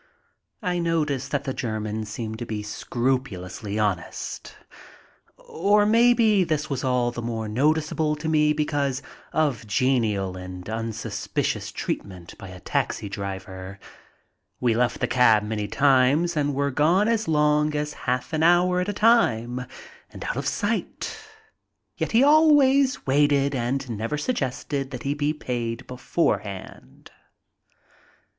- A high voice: No, low, 135 Hz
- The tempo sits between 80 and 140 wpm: Yes, slow, 135 wpm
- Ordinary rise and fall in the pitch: No, wide, 5.9 semitones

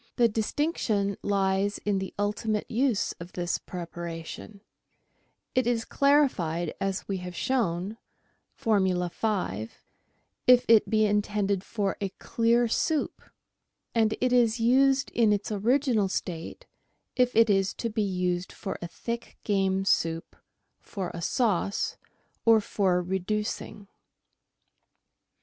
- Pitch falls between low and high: No, high, 205 Hz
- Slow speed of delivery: Yes, slow, 125 wpm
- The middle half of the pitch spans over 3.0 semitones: Yes, average, 3.6 semitones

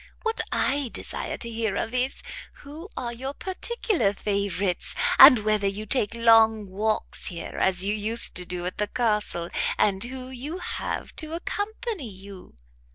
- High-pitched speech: Yes, high, 225 Hz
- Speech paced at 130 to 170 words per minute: Yes, average, 160 wpm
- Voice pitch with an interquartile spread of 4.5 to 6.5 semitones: Yes, average, 5.1 semitones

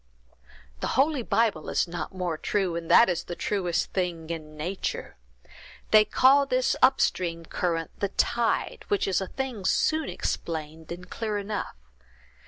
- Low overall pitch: No, medium, 185 Hz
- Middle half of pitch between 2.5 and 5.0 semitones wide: No, wide, 5.5 semitones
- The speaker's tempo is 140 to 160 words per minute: Yes, average, 155 wpm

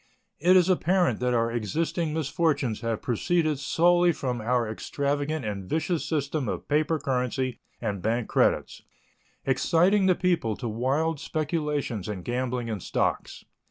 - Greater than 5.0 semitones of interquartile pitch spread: Yes, wide, 5.5 semitones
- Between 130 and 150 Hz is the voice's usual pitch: Yes, medium, 140 Hz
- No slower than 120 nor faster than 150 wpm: Yes, average, 140 wpm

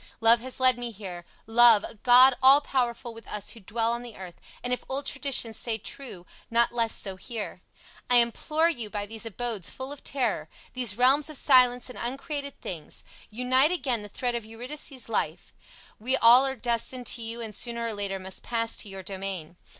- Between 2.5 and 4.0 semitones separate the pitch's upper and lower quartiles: Yes, average, 3.2 semitones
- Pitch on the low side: No, high, 235 Hz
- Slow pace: No, average, 195 wpm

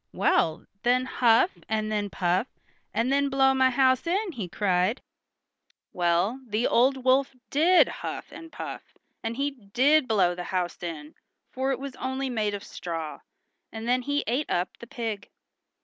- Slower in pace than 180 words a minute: Yes, average, 165 wpm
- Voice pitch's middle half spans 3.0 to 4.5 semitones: No, average, 5.3 semitones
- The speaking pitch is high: Yes, high, 240 Hz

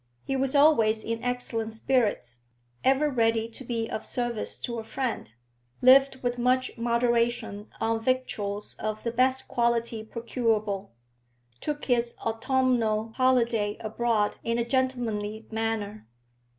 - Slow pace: Yes, slow, 125 wpm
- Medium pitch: No, high, 235 Hz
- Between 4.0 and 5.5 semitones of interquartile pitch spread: No, narrow, 2.5 semitones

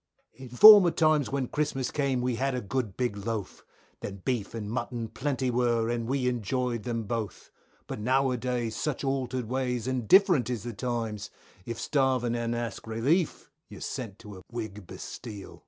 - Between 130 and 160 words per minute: No, average, 175 wpm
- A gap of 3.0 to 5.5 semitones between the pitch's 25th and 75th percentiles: No, narrow, 2.5 semitones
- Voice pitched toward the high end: No, low, 120 Hz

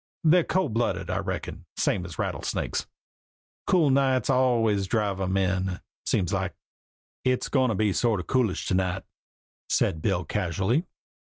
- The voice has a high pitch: No, low, 105 Hz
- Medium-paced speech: Yes, average, 155 wpm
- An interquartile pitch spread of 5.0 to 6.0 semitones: Yes, wide, 5.4 semitones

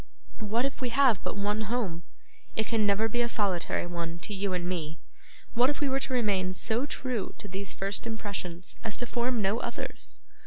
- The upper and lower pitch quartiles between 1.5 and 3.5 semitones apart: No, average, 4.2 semitones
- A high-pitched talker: Yes, high, 210 Hz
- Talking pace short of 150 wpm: No, average, 200 wpm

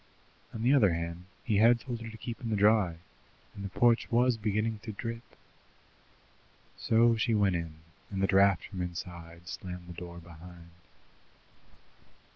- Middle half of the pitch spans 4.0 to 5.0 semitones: Yes, average, 4.5 semitones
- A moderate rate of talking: Yes, average, 160 wpm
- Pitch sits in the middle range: No, low, 100 Hz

